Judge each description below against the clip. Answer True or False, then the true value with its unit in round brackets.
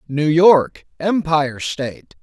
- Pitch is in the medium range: True (155 Hz)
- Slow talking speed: True (110 wpm)